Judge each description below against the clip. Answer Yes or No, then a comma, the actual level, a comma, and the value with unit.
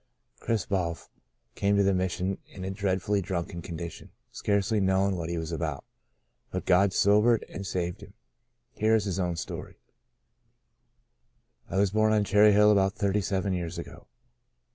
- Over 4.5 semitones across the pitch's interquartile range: No, narrow, 2.5 semitones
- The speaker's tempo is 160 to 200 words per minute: Yes, average, 165 wpm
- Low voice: Yes, very low, 95 Hz